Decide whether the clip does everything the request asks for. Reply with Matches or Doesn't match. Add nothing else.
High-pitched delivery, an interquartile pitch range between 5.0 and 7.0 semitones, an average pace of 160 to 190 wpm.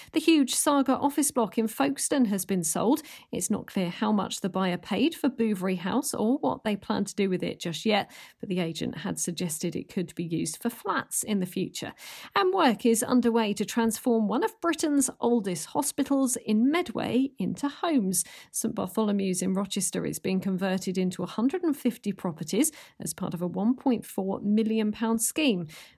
Matches